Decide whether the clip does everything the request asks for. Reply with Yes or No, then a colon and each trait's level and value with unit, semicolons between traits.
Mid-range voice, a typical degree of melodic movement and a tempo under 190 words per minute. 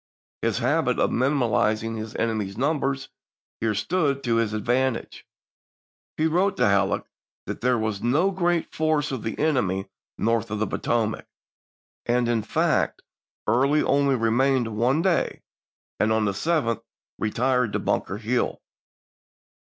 No: low, 120 Hz; average, 4.3 semitones; average, 140 wpm